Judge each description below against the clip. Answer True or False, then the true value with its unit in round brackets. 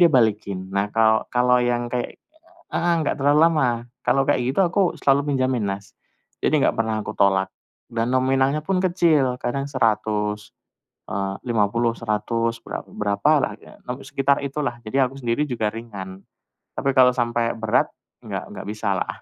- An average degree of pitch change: True (4.2 semitones)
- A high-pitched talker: False (120 Hz)